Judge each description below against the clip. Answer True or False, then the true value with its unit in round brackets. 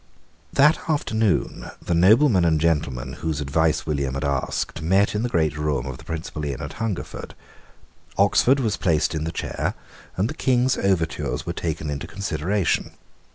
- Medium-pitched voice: False (80 Hz)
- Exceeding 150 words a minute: True (160 wpm)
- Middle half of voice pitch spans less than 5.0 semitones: False (5.6 semitones)